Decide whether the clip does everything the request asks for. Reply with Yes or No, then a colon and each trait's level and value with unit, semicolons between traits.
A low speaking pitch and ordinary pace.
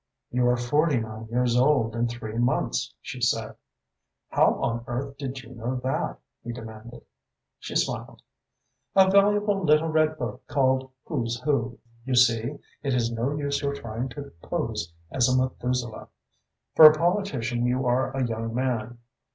Yes: low, 125 Hz; average, 160 wpm